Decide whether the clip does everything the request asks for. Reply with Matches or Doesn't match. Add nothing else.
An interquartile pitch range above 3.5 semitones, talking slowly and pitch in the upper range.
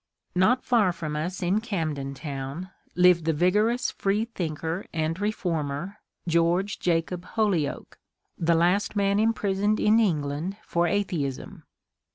Doesn't match